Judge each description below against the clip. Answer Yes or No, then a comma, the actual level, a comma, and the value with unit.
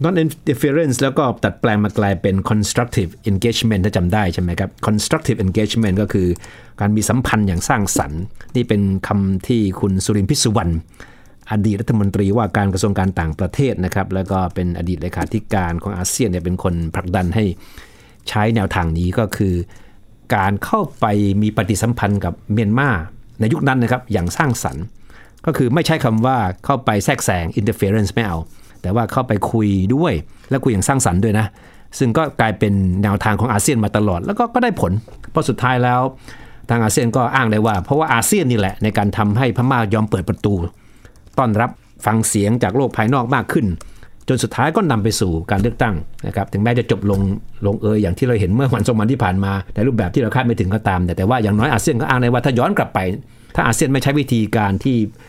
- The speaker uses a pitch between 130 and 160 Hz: No, low, 110 Hz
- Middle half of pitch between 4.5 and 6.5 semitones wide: No, average, 3.7 semitones